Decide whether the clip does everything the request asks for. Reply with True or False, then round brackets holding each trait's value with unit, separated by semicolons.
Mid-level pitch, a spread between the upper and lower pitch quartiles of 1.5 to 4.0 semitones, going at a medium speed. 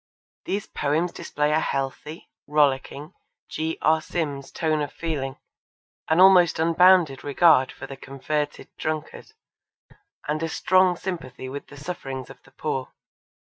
False (150 Hz; 3.4 semitones; 130 wpm)